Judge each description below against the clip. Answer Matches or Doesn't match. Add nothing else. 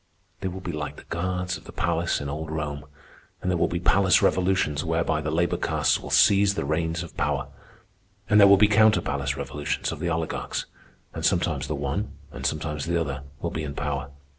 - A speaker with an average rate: Doesn't match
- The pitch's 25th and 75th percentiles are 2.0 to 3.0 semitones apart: Doesn't match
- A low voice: Matches